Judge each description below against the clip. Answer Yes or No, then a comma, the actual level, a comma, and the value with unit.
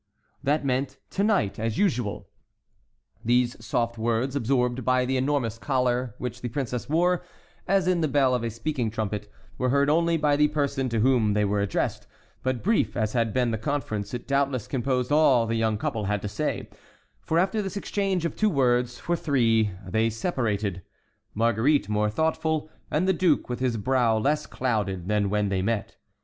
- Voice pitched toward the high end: No, low, 125 Hz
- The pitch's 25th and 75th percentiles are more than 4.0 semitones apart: Yes, average, 4.7 semitones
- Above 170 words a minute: Yes, average, 185 wpm